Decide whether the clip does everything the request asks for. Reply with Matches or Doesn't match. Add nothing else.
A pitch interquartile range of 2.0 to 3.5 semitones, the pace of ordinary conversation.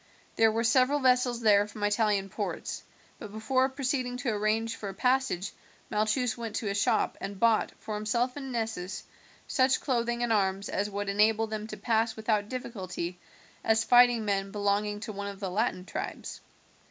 Matches